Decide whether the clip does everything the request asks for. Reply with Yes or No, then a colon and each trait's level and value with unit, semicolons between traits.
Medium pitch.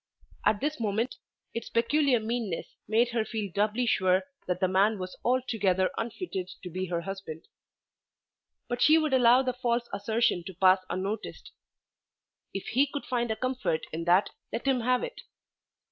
No: high, 220 Hz